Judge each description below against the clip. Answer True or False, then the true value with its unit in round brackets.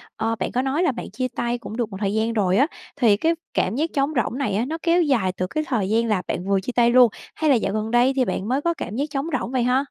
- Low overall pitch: False (240 Hz)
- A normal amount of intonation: True (4.2 semitones)